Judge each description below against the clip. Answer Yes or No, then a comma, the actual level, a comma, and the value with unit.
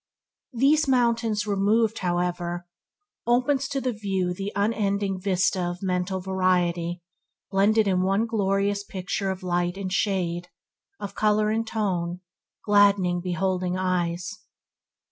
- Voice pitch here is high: Yes, high, 195 Hz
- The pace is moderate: No, slow, 125 wpm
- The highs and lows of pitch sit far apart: No, average, 2.9 semitones